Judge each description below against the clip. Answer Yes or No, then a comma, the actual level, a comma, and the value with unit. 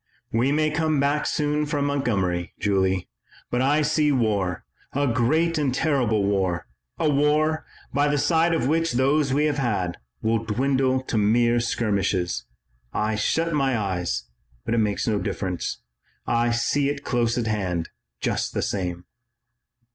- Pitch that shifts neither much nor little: No, wide, 6.0 semitones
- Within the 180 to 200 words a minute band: No, average, 155 wpm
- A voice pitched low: Yes, low, 125 Hz